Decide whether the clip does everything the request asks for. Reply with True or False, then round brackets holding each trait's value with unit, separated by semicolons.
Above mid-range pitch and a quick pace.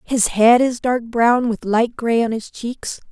True (235 Hz; 210 wpm)